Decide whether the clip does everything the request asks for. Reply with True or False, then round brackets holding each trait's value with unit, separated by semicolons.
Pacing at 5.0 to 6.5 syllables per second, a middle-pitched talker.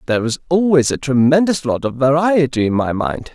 True (5.5 syllables/s; 145 Hz)